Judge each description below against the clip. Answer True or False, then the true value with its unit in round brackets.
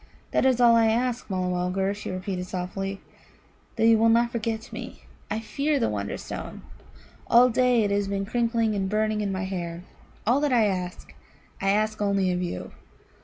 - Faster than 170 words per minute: True (180 wpm)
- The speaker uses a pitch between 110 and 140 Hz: False (210 Hz)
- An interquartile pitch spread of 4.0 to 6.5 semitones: False (3.4 semitones)